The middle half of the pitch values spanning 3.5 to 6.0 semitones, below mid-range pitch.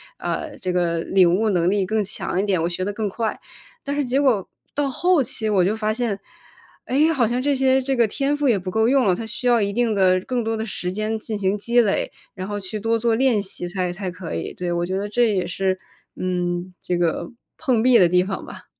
No: average, 4.6 semitones; high, 210 Hz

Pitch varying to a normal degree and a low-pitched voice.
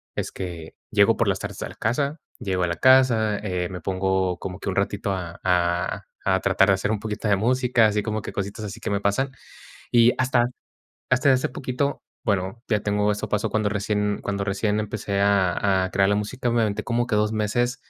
Yes: average, 3.2 semitones; low, 105 Hz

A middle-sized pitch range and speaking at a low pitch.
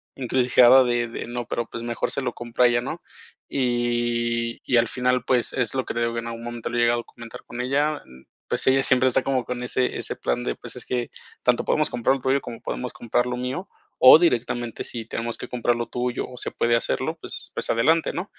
No: narrow, 1.4 semitones; low, 120 Hz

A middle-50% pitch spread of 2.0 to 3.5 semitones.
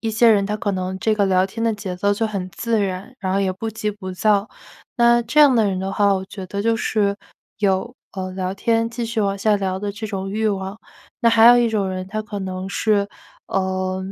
Yes: average, 2.8 semitones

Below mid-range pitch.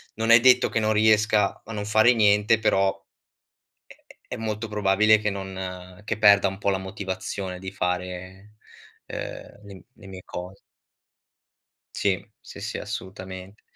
Yes: low, 100 Hz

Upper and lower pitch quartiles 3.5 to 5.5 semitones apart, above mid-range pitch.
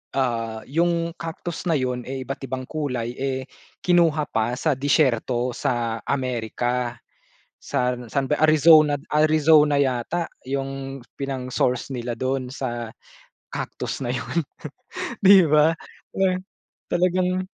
No: average, 3.9 semitones; low, 135 Hz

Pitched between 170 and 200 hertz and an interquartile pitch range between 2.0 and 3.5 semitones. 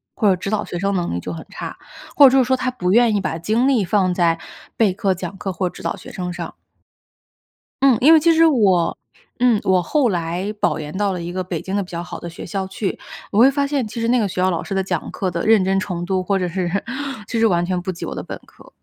No: high, 190 Hz; average, 4.1 semitones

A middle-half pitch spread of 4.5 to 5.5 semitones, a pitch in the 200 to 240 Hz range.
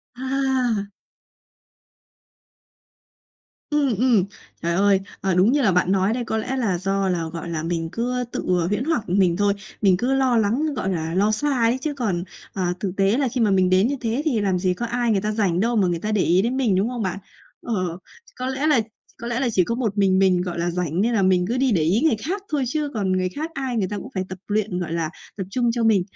Yes: average, 5.0 semitones; high, 210 Hz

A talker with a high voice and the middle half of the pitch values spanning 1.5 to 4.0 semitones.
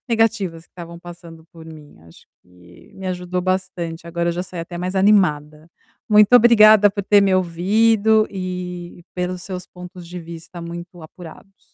No: medium, 180 Hz; narrow, 2.5 semitones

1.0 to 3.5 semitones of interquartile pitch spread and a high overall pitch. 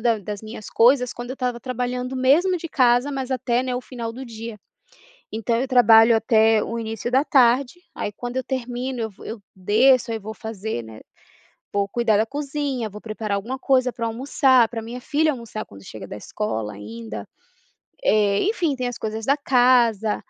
Yes: average, 3.0 semitones; high, 235 Hz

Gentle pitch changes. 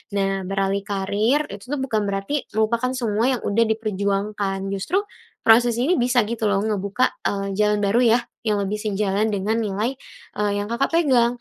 No: average, 3.1 semitones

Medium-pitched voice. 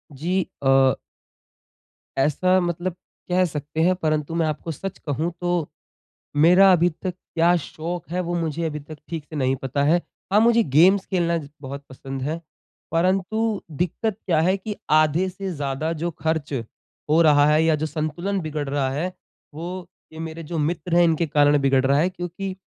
Yes: medium, 165 Hz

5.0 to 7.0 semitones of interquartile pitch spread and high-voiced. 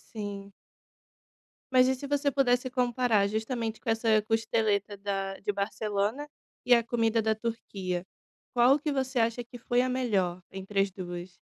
No: average, 3.7 semitones; high, 225 Hz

